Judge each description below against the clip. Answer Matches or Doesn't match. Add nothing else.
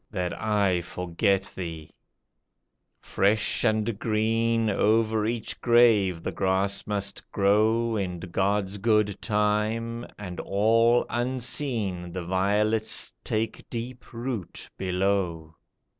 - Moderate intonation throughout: Matches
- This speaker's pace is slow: Matches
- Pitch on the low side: Matches